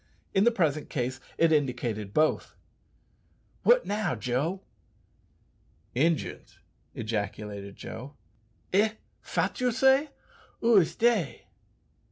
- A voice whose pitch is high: No, medium, 155 Hz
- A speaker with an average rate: No, slow, 100 wpm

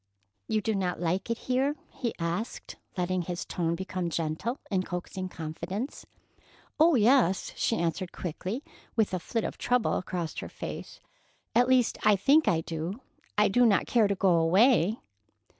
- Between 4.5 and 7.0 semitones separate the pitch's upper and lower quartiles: Yes, average, 5.0 semitones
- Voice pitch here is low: No, high, 190 Hz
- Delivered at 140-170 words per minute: Yes, average, 160 wpm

